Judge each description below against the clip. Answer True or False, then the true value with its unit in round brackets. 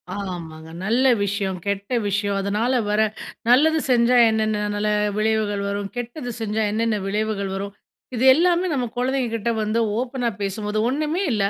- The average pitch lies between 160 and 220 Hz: True (215 Hz)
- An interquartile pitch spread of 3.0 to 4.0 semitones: True (3.4 semitones)